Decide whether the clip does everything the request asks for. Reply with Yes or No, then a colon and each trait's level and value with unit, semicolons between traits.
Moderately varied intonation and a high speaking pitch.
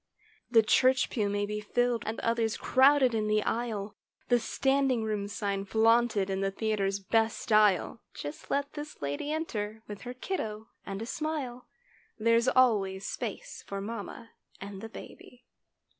Yes: average, 3.2 semitones; high, 220 Hz